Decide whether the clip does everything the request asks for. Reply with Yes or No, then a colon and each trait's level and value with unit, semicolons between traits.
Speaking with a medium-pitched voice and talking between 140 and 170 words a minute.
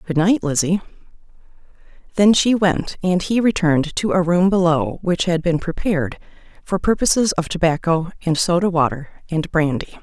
Yes: medium, 175 Hz; average, 155 wpm